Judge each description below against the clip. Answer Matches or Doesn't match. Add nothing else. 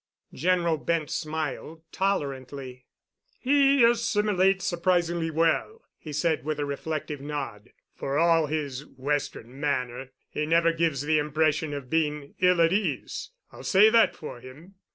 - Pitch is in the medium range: Matches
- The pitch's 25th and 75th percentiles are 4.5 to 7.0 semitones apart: Doesn't match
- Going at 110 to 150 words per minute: Matches